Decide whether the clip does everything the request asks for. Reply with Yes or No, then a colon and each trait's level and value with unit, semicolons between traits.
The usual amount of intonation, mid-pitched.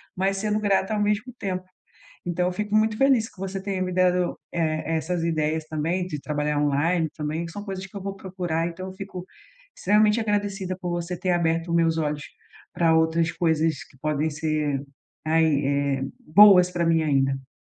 Yes: average, 3.5 semitones; medium, 175 Hz